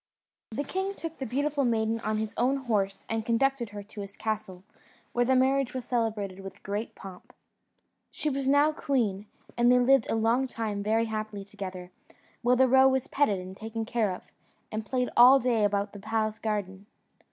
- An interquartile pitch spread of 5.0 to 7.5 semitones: No, average, 4.0 semitones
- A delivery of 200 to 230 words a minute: No, average, 185 wpm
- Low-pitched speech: No, high, 225 Hz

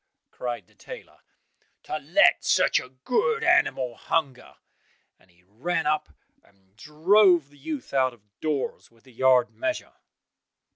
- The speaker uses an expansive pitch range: Yes, wide, 6.6 semitones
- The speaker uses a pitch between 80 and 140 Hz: Yes, low, 135 Hz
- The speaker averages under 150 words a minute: Yes, average, 140 wpm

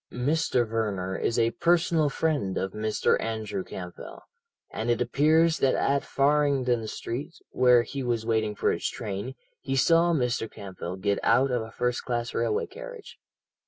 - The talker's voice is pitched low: Yes, low, 120 Hz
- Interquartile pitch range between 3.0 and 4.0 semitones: No, average, 4.5 semitones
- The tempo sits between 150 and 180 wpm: Yes, average, 160 wpm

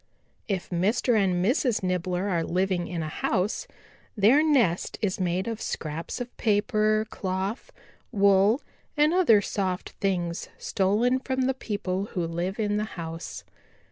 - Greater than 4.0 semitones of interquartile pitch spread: No, average, 3.6 semitones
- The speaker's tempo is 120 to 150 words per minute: Yes, average, 140 wpm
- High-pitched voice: Yes, high, 195 Hz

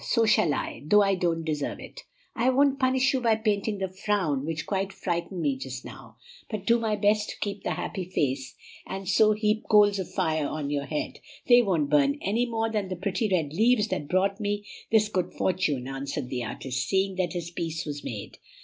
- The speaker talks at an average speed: No, fast, 210 wpm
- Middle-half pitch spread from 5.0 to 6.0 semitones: Yes, average, 5.3 semitones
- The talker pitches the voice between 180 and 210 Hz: Yes, high, 190 Hz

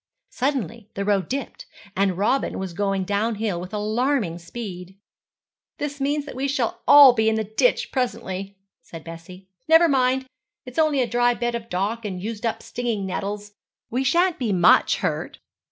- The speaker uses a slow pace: No, average, 170 wpm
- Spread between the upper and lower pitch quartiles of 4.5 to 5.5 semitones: Yes, average, 4.9 semitones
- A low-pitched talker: No, high, 220 Hz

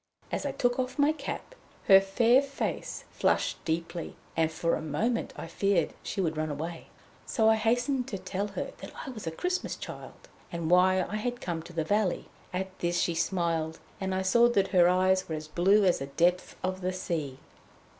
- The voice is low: No, medium, 185 Hz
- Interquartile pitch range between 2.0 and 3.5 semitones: No, average, 4.6 semitones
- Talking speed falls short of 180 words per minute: No, average, 200 wpm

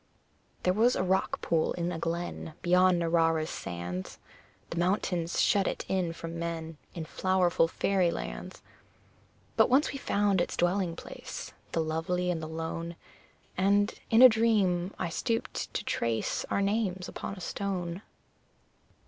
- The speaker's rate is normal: Yes, average, 150 wpm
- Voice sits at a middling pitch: Yes, medium, 175 Hz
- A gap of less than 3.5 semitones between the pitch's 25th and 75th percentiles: Yes, average, 2.8 semitones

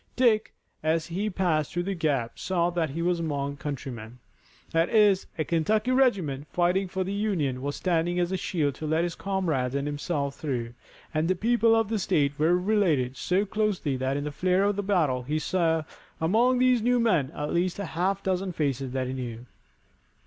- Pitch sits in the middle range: Yes, medium, 170 Hz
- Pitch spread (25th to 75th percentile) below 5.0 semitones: No, average, 5.3 semitones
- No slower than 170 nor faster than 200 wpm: Yes, average, 195 wpm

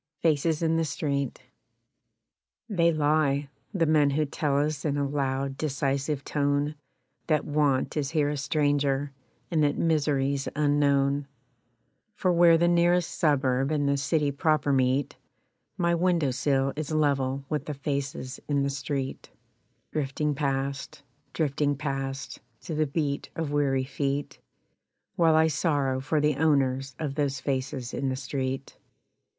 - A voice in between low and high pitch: Yes, medium, 145 Hz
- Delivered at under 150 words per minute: Yes, average, 140 wpm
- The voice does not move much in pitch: Yes, narrow, 2.0 semitones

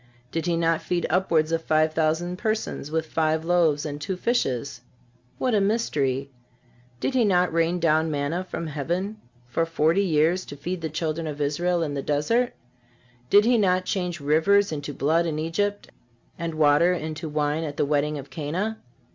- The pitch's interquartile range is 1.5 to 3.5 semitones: Yes, average, 3.2 semitones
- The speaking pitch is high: No, medium, 165 Hz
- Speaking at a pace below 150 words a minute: No, average, 175 wpm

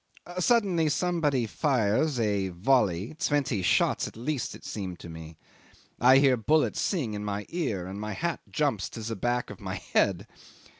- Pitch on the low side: Yes, low, 120 Hz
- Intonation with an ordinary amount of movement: No, wide, 6.7 semitones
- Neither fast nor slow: Yes, average, 165 wpm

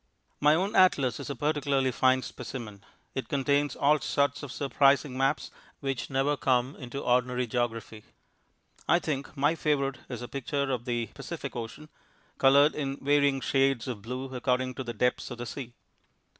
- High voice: No, low, 135 Hz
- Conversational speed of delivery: Yes, average, 165 wpm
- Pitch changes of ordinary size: No, narrow, 2.3 semitones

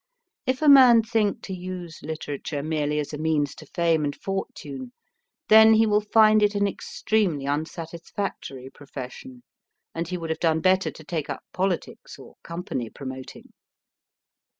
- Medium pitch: Yes, medium, 170 Hz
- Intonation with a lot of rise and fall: Yes, wide, 6.0 semitones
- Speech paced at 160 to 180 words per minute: No, average, 150 wpm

